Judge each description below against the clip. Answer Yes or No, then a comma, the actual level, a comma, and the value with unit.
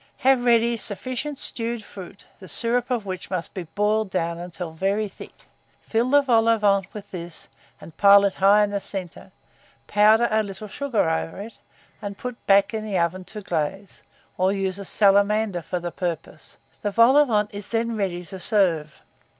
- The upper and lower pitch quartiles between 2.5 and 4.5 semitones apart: Yes, average, 3.2 semitones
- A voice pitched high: Yes, high, 200 Hz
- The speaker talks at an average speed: Yes, average, 190 wpm